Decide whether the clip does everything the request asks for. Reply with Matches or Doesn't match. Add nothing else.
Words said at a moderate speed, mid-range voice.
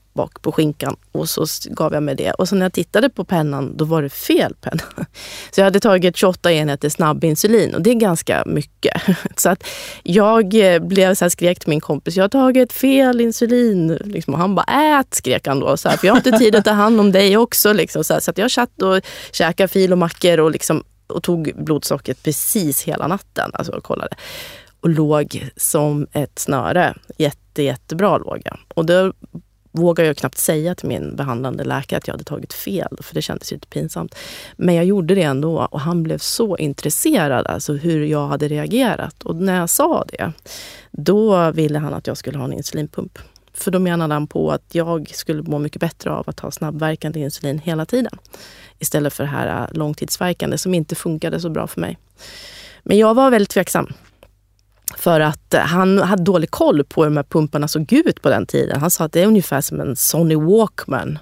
Doesn't match